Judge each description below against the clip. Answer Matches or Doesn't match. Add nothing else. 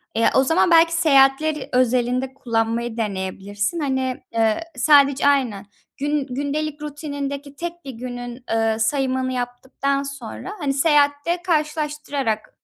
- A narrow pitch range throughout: Doesn't match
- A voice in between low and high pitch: Doesn't match